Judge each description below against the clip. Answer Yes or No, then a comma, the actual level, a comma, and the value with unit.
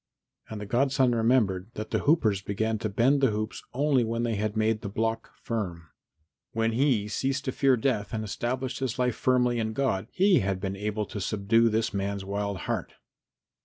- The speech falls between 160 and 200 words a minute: Yes, average, 190 wpm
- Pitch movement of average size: Yes, average, 3.5 semitones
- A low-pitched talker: Yes, low, 110 Hz